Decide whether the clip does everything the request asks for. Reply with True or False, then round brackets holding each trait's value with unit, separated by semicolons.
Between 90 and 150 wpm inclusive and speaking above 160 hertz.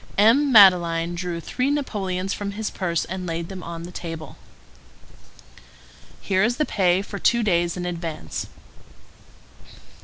True (140 wpm; 185 Hz)